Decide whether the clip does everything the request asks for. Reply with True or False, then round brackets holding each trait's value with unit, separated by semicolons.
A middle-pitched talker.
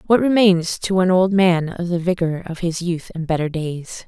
True (175 Hz)